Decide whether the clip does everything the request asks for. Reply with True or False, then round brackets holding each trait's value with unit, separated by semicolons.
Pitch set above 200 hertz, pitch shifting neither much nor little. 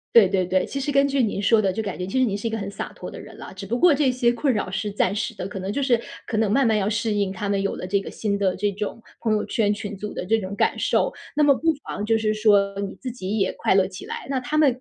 True (210 Hz; 3.3 semitones)